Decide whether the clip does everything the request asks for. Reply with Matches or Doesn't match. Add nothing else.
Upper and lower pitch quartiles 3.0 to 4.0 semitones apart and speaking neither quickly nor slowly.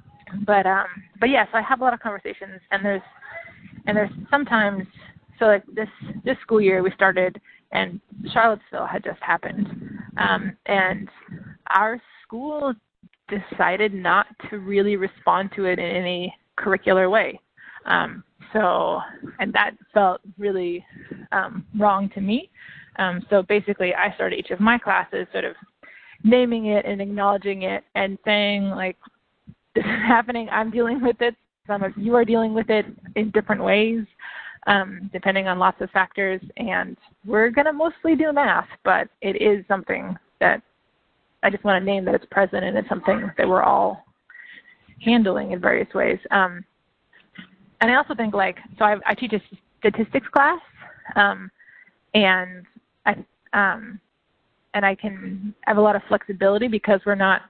Doesn't match